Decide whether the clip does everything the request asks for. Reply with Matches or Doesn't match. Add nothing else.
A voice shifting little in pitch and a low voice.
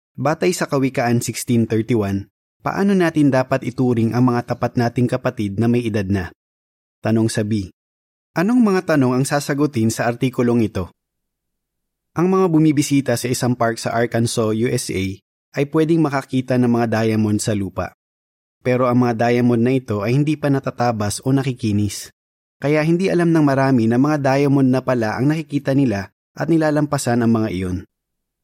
Doesn't match